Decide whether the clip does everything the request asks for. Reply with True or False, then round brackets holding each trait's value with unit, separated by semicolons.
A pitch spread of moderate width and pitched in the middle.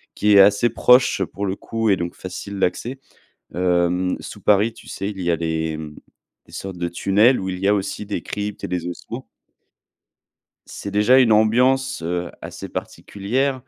False (3.8 semitones; 100 Hz)